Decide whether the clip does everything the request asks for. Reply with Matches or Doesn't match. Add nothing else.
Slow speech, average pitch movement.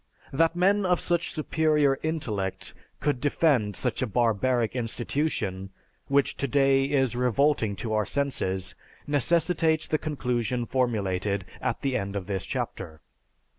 Doesn't match